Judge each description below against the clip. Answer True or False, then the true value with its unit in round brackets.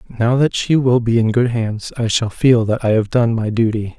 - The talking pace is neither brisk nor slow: False (255 wpm)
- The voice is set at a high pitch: False (115 Hz)